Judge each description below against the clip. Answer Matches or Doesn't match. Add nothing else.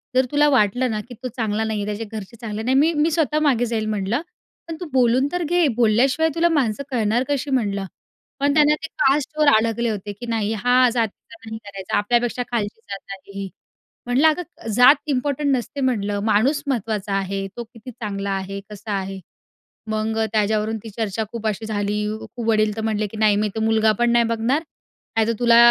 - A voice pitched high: Matches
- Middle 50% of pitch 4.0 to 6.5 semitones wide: Doesn't match